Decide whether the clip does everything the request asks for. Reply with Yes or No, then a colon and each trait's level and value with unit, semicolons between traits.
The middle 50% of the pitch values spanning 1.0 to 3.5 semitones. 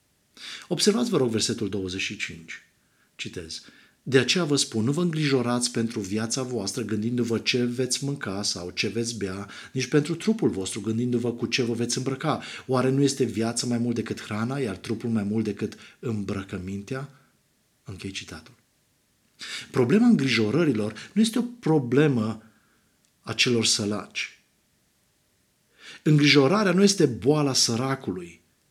No: average, 4.2 semitones